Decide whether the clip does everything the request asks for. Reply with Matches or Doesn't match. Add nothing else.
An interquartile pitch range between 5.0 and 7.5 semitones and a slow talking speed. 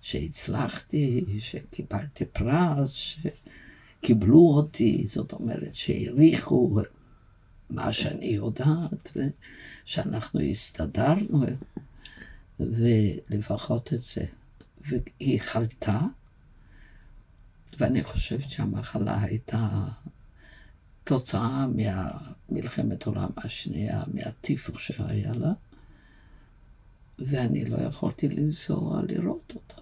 Matches